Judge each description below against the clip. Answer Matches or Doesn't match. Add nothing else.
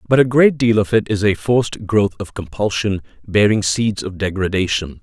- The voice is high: Doesn't match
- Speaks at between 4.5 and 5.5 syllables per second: Matches